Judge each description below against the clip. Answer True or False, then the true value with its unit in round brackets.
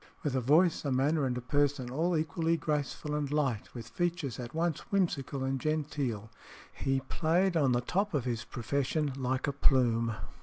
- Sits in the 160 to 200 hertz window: False (140 Hz)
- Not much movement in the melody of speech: False (3.8 semitones)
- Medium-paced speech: True (180 wpm)